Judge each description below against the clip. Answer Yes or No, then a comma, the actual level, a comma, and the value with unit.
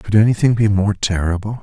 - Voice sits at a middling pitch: No, low, 105 Hz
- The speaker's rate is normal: Yes, average, 185 wpm